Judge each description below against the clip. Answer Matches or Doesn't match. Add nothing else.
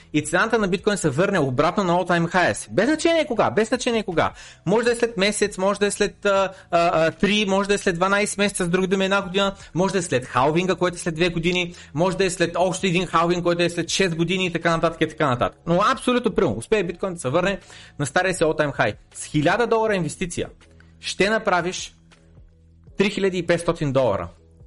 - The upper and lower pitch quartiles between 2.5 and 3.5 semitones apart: Doesn't match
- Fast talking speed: Matches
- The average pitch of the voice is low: Doesn't match